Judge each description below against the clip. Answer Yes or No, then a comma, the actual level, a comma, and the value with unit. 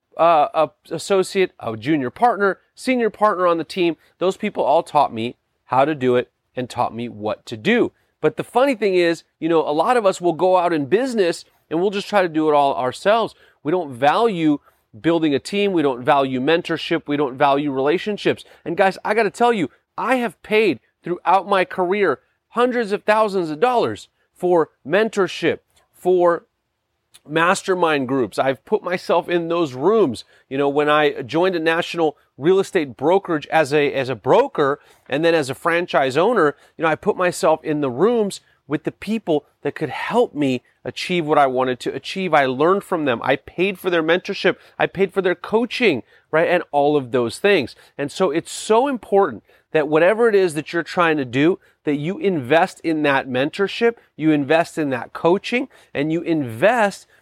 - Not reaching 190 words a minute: No, average, 195 wpm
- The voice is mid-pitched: Yes, medium, 165 Hz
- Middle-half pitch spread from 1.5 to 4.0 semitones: No, average, 4.9 semitones